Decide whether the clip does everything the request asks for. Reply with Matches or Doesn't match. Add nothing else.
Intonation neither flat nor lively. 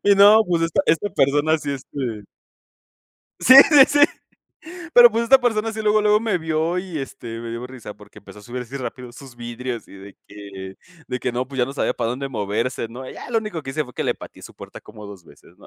Doesn't match